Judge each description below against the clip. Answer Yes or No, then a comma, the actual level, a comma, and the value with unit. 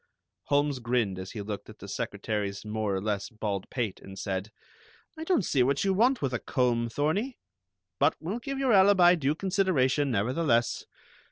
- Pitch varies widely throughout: Yes, wide, 9.0 semitones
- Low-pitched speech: Yes, low, 130 Hz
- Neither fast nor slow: Yes, average, 175 wpm